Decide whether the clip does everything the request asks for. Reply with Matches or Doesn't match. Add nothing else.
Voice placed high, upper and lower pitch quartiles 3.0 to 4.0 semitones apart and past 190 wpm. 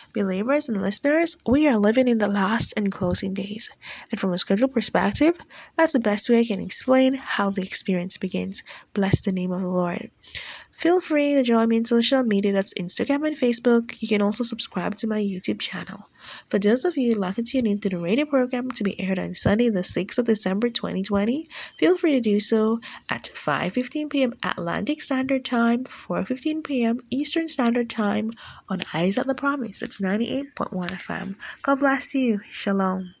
Doesn't match